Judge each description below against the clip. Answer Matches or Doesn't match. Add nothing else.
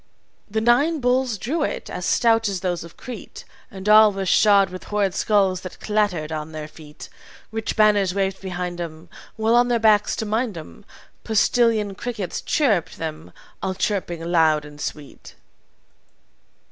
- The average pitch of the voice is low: Doesn't match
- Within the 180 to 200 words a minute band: Doesn't match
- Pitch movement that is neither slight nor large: Matches